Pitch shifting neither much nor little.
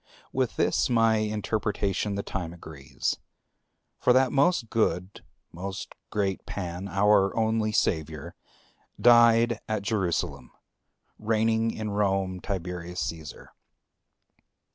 Yes: average, 3.6 semitones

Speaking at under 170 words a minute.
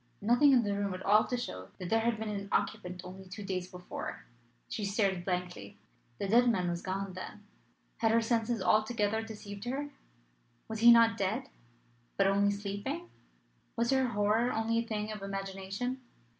No: average, 175 wpm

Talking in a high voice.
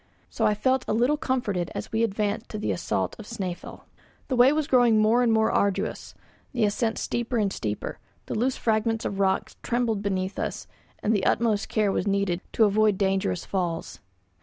Yes: high, 215 Hz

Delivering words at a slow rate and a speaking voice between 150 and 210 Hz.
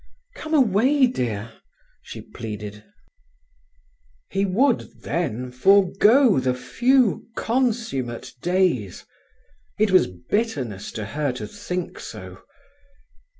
Yes: slow, 95 wpm; medium, 185 Hz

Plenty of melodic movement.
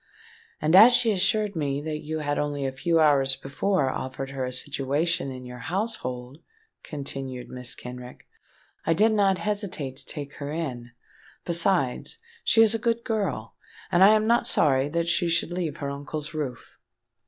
Yes: wide, 5.7 semitones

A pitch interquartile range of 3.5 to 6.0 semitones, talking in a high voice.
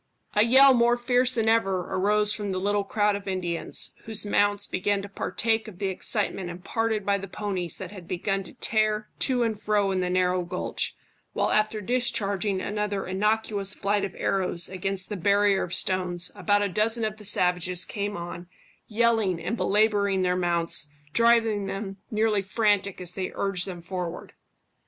No: narrow, 2.5 semitones; high, 200 Hz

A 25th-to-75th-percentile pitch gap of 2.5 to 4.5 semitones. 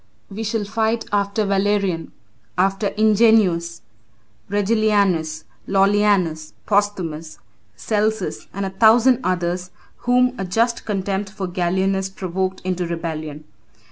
Yes: average, 2.9 semitones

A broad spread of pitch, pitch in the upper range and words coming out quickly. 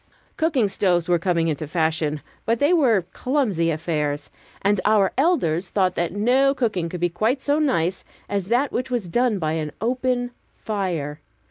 No: wide, 6.9 semitones; high, 195 Hz; average, 165 wpm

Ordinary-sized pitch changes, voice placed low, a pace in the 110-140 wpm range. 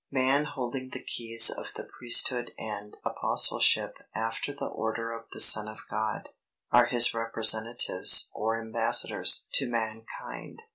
No: narrow, 1.7 semitones; low, 115 Hz; slow, 135 wpm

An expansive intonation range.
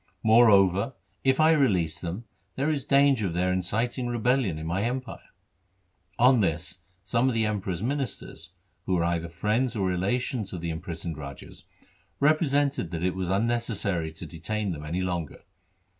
Yes: wide, 6.2 semitones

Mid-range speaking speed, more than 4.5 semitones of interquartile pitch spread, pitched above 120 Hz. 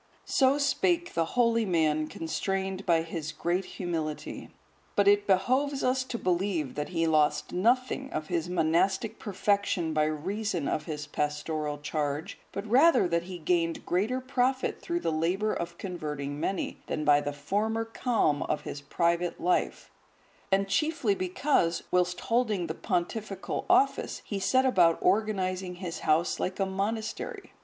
Yes: average, 150 wpm; average, 5.2 semitones; medium, 185 Hz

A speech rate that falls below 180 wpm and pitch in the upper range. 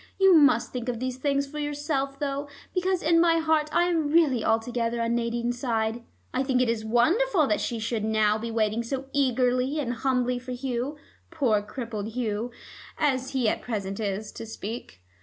No: average, 185 wpm; very high, 250 Hz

